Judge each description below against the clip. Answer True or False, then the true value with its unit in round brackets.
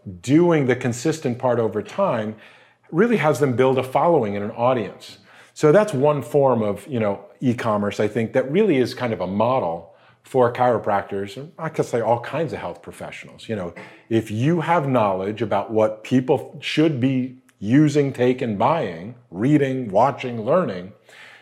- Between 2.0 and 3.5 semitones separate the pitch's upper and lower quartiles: False (5.1 semitones)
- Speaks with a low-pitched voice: True (125 Hz)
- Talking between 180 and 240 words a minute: False (170 wpm)